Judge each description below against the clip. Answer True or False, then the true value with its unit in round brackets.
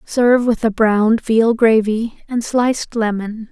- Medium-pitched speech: False (225 Hz)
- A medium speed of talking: True (155 wpm)